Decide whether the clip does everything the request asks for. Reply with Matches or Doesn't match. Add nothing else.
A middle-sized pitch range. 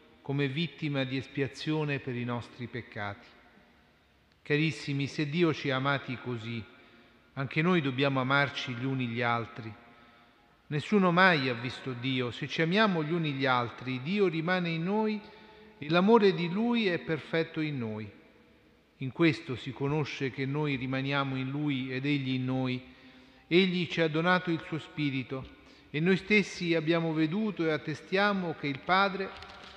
Matches